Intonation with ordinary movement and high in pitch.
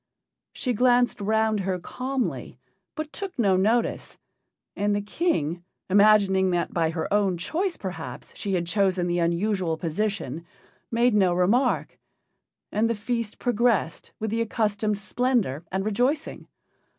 Yes: average, 4.4 semitones; high, 205 Hz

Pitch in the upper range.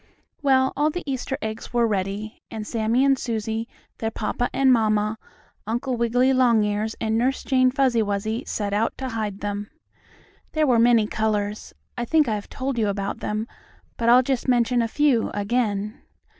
Yes: high, 230 Hz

